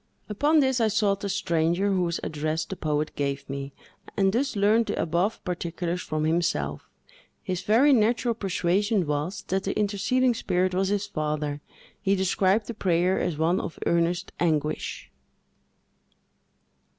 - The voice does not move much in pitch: No, average, 3.9 semitones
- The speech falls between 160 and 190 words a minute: No, average, 145 wpm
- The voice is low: No, medium, 185 Hz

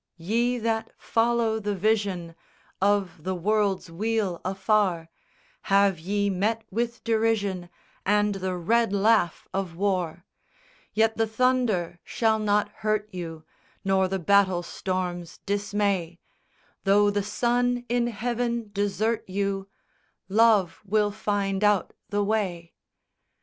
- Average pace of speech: No, slow, 125 wpm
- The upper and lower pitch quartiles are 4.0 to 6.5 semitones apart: No, average, 2.9 semitones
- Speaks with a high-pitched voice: Yes, high, 205 Hz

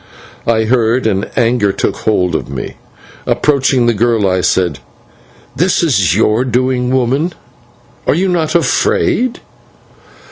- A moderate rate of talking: No, slow, 130 wpm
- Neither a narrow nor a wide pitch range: Yes, average, 4.7 semitones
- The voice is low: Yes, low, 120 Hz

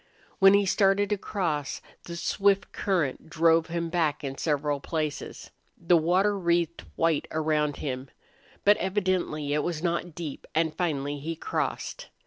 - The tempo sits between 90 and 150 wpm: Yes, average, 145 wpm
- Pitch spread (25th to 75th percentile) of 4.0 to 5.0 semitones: No, average, 3.5 semitones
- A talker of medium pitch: Yes, medium, 165 Hz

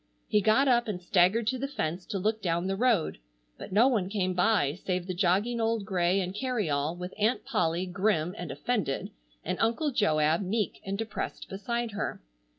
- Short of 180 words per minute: No, average, 185 wpm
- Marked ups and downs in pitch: No, average, 4.1 semitones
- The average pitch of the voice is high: Yes, high, 195 Hz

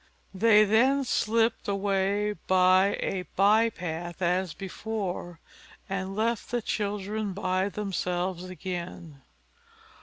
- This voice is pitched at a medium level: No, high, 195 Hz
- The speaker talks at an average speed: No, slow, 100 wpm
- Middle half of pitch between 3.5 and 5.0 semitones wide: No, narrow, 2.5 semitones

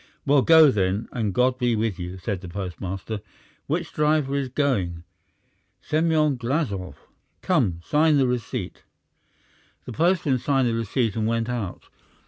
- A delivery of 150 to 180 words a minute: No, average, 140 wpm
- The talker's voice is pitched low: Yes, low, 120 Hz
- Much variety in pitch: Yes, wide, 6.1 semitones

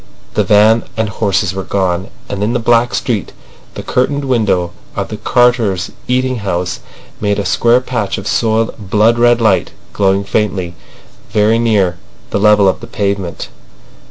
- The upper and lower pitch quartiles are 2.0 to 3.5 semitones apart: Yes, average, 3.2 semitones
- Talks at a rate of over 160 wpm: No, average, 155 wpm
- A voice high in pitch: No, low, 105 Hz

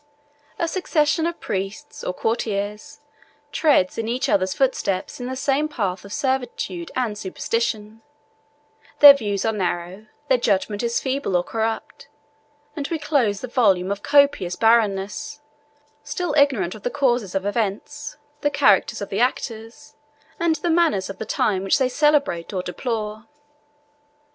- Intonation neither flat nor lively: No, wide, 6.0 semitones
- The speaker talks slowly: No, average, 150 wpm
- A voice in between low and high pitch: No, high, 225 Hz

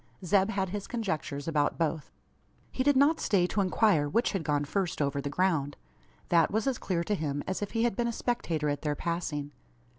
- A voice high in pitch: No, medium, 175 Hz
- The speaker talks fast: Yes, fast, 210 wpm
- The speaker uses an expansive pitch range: Yes, wide, 6.0 semitones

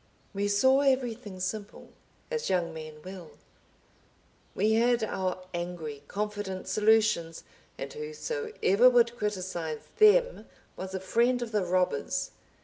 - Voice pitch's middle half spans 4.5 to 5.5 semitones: Yes, average, 4.9 semitones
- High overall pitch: Yes, high, 205 Hz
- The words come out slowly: Yes, slow, 120 wpm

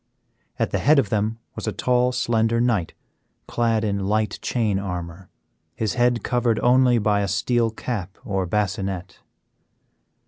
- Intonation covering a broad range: No, average, 3.6 semitones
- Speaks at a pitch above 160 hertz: No, low, 110 Hz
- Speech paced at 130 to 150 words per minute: Yes, average, 145 wpm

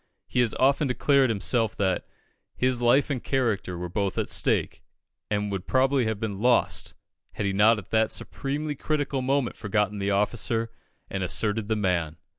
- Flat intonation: No, average, 4.4 semitones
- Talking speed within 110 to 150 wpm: No, average, 170 wpm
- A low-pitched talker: Yes, low, 110 Hz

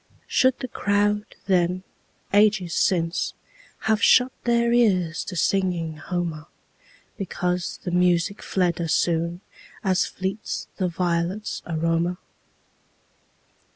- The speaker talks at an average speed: No, slow, 90 wpm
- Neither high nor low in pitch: Yes, medium, 180 Hz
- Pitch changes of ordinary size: Yes, average, 3.3 semitones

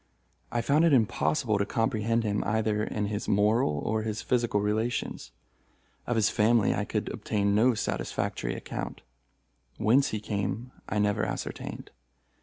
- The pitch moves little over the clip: Yes, narrow, 2.1 semitones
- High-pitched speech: No, low, 110 Hz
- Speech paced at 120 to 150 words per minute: Yes, average, 145 wpm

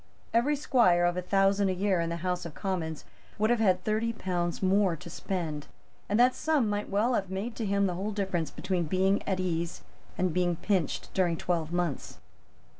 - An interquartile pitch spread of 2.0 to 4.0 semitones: Yes, average, 2.9 semitones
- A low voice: No, medium, 185 Hz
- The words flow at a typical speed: Yes, average, 195 wpm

